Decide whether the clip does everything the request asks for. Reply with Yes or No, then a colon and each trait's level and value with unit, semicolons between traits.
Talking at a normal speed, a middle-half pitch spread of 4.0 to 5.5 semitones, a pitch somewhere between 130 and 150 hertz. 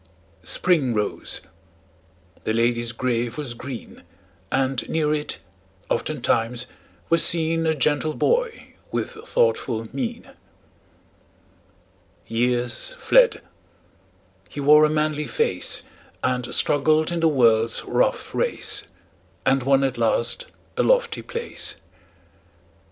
No: slow, 105 wpm; average, 5.2 semitones; medium, 140 Hz